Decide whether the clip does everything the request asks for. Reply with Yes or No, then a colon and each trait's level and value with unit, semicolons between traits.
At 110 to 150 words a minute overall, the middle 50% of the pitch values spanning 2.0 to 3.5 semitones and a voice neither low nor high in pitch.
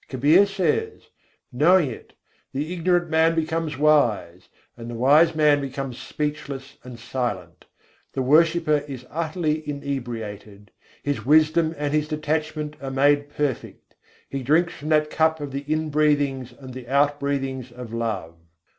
Yes: slow, 135 wpm; average, 3.2 semitones; medium, 145 Hz